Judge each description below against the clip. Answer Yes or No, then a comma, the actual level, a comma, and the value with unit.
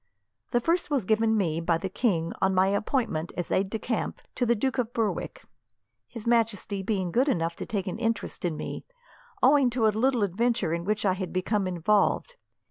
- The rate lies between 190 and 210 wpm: Yes, average, 200 wpm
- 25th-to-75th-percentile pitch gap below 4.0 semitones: No, average, 4.4 semitones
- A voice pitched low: No, high, 210 Hz